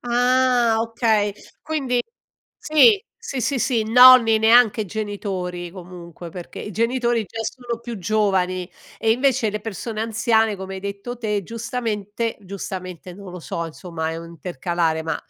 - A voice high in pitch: Yes, high, 215 Hz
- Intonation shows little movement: No, average, 4.5 semitones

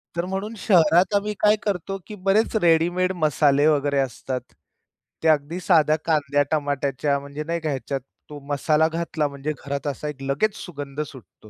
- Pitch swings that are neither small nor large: Yes, average, 3.5 semitones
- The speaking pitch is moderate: Yes, medium, 150 Hz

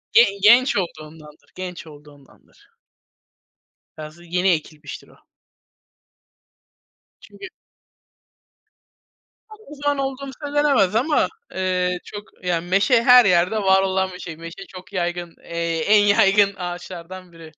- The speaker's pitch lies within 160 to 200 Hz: Yes, medium, 185 Hz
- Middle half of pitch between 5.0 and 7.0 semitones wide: No, average, 3.9 semitones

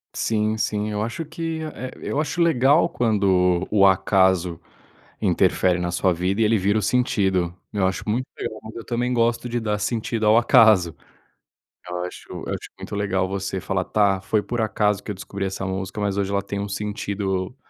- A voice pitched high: No, low, 105 Hz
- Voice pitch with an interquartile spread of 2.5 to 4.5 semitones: Yes, average, 3.0 semitones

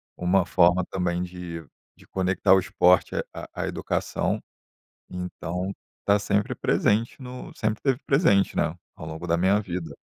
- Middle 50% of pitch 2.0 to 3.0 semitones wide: Yes, narrow, 2.4 semitones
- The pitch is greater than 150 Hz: No, very low, 90 Hz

